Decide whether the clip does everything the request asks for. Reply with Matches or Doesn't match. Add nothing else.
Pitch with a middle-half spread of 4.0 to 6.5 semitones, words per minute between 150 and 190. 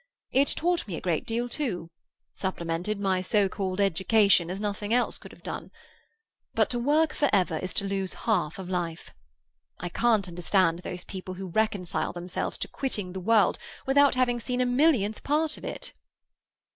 Matches